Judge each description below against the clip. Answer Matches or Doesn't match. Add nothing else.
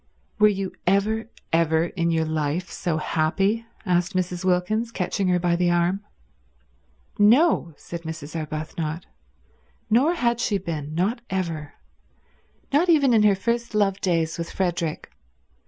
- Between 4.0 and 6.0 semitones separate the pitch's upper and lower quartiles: Matches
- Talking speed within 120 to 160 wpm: Matches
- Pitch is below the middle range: Doesn't match